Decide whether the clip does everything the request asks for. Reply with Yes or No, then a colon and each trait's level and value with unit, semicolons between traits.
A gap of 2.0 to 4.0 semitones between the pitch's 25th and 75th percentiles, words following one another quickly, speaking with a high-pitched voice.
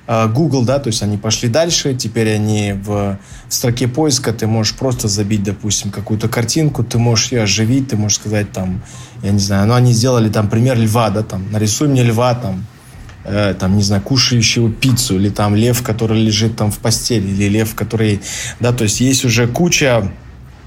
No: average, 2.8 semitones; fast, 190 wpm; low, 110 Hz